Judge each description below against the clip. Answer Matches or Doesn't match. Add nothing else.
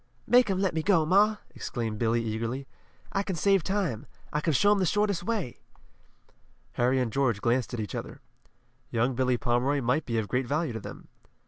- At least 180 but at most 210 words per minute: Matches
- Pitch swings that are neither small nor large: Doesn't match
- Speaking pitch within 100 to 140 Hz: Matches